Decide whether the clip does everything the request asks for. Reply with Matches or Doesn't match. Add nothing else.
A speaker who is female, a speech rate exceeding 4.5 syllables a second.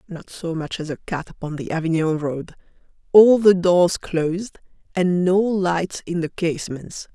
Doesn't match